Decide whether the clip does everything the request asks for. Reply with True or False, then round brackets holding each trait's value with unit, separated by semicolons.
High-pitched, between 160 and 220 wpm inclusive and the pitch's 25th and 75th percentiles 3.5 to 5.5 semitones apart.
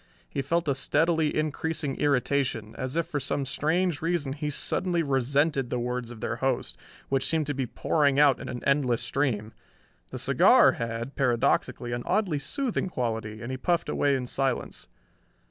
False (140 Hz; 170 wpm; 3.9 semitones)